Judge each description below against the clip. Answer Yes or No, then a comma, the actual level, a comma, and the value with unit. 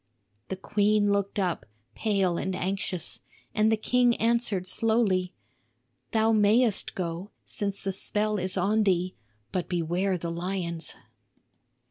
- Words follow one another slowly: Yes, slow, 125 wpm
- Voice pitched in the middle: No, high, 195 Hz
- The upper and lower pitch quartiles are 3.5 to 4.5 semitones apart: No, average, 2.8 semitones